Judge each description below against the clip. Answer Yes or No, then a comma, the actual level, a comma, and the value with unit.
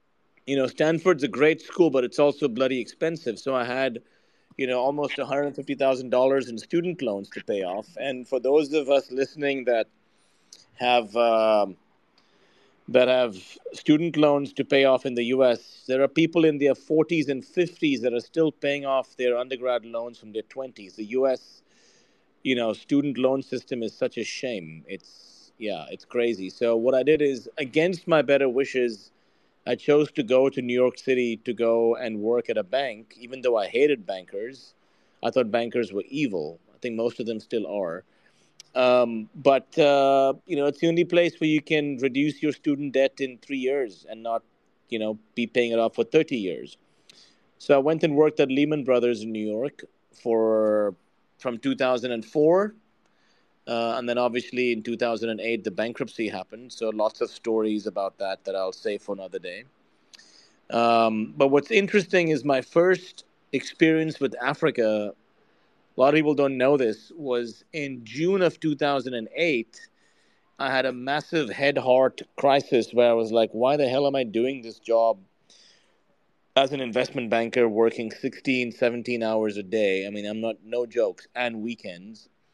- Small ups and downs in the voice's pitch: No, average, 3.7 semitones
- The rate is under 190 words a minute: Yes, average, 175 wpm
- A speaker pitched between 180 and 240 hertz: No, low, 130 Hz